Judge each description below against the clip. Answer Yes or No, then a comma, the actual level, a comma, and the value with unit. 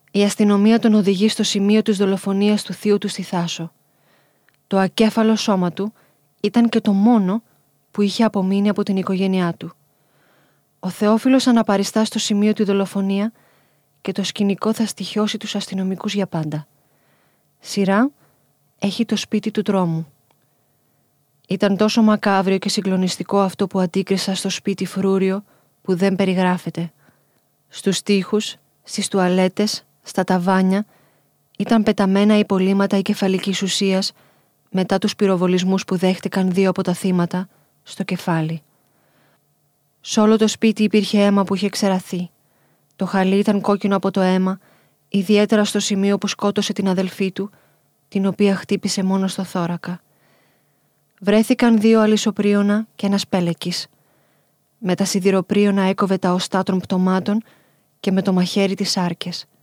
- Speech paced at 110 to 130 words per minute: No, average, 140 wpm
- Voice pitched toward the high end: Yes, high, 195 Hz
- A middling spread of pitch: No, narrow, 1.9 semitones